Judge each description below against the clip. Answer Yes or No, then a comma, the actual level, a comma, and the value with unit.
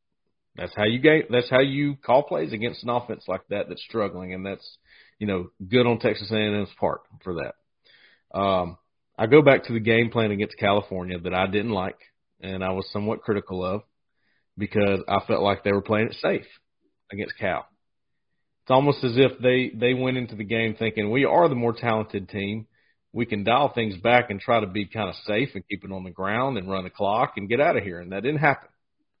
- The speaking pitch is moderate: No, low, 110 Hz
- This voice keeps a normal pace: No, fast, 220 wpm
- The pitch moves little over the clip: No, average, 3.6 semitones